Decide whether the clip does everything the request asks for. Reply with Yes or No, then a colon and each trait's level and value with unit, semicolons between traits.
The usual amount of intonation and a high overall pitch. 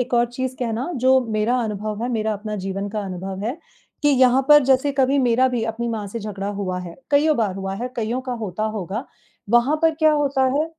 Yes: average, 4.2 semitones; high, 235 Hz